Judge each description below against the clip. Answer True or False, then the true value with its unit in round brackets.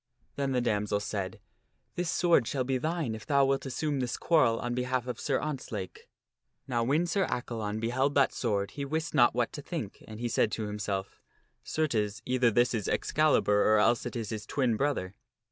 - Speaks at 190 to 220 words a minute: True (200 wpm)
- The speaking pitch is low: True (120 Hz)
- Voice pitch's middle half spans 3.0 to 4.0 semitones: False (4.4 semitones)